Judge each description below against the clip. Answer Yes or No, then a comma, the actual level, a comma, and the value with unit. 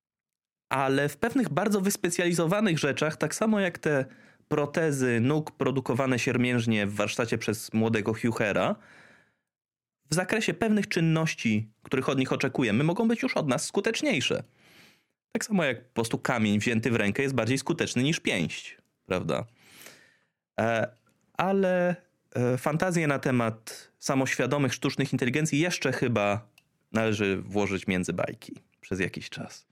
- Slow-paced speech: No, average, 130 wpm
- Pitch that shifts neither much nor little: No, wide, 6.9 semitones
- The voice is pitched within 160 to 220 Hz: No, medium, 140 Hz